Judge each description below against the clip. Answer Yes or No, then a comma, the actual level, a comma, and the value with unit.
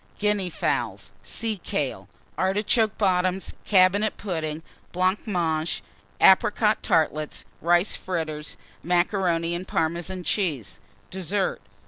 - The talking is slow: Yes, slow, 90 wpm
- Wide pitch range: No, average, 3.2 semitones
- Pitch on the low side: No, medium, 180 Hz